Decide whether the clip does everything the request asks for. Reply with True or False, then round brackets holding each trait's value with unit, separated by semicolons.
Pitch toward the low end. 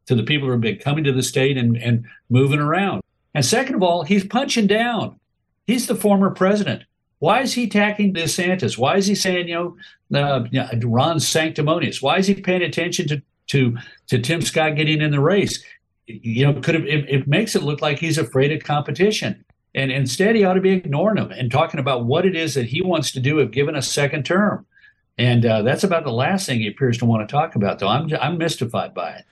False (155 Hz)